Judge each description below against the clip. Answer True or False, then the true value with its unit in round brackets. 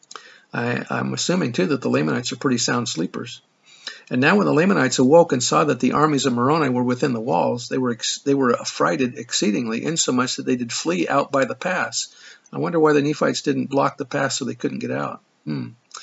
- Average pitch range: True (3.3 semitones)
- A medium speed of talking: False (220 wpm)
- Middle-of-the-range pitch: False (130 Hz)